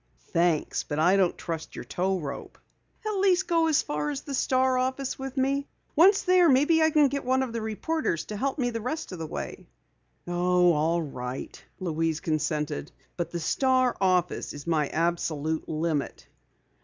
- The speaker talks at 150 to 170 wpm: No, average, 180 wpm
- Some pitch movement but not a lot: No, wide, 9.0 semitones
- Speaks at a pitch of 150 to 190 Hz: Yes, medium, 185 Hz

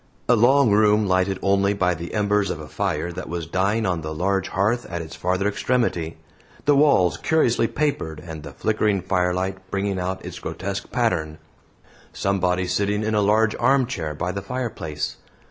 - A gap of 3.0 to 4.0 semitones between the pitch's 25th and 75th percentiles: Yes, average, 3.3 semitones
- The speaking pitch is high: No, low, 100 Hz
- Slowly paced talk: No, average, 170 wpm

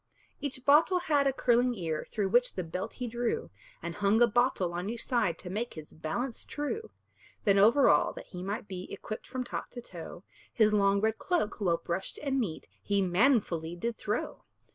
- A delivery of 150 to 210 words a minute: Yes, average, 195 wpm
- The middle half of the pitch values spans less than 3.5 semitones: No, average, 5.2 semitones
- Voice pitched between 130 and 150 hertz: No, high, 215 Hz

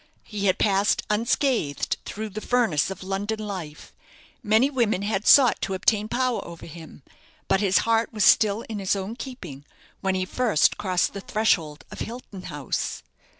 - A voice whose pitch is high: Yes, high, 205 Hz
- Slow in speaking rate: No, average, 165 wpm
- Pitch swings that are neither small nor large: Yes, average, 3.2 semitones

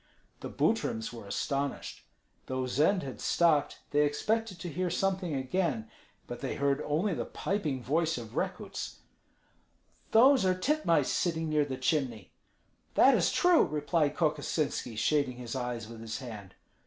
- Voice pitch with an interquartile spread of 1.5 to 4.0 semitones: No, wide, 5.4 semitones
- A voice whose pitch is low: No, medium, 145 Hz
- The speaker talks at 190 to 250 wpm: No, average, 145 wpm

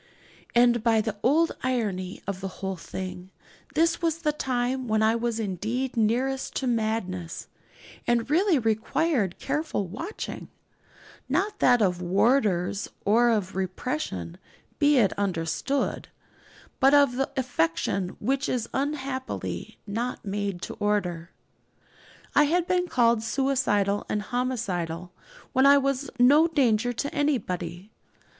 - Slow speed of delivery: Yes, slow, 125 wpm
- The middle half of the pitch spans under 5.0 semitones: No, wide, 5.6 semitones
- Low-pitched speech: No, high, 235 Hz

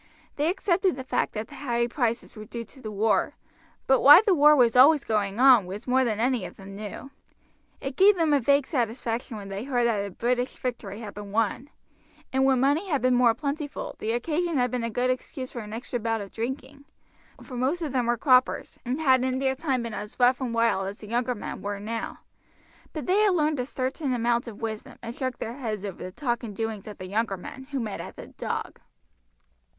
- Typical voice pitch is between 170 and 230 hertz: No, high, 245 Hz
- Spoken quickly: Yes, fast, 230 wpm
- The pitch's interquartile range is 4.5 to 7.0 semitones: No, average, 3.4 semitones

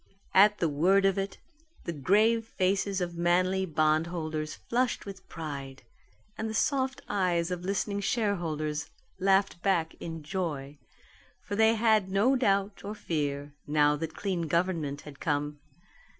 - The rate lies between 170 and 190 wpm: No, average, 140 wpm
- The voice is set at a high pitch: No, medium, 180 Hz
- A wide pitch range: No, average, 4.4 semitones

